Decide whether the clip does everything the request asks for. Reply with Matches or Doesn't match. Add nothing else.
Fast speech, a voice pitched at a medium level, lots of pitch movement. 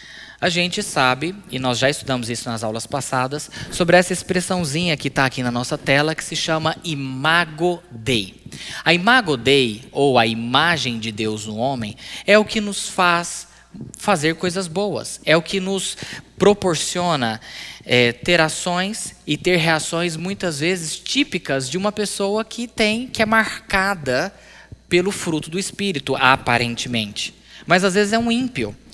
Doesn't match